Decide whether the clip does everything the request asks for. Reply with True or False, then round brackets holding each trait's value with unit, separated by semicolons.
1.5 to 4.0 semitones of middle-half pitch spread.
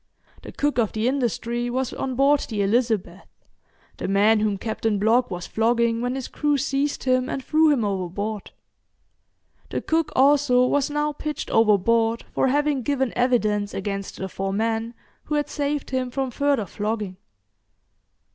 False (4.4 semitones)